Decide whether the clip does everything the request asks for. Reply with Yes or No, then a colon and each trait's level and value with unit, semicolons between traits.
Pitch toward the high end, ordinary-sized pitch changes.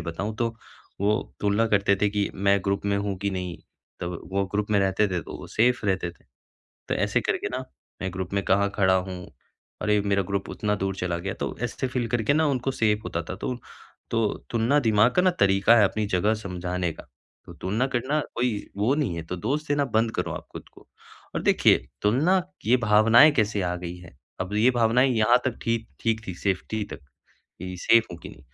No: low, 105 Hz; average, 3.5 semitones